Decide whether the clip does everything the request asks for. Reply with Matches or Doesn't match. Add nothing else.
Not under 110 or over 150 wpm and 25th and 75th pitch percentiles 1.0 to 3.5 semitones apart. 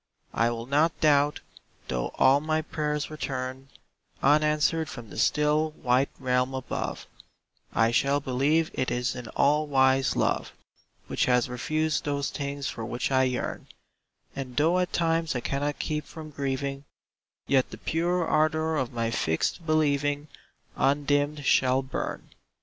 Matches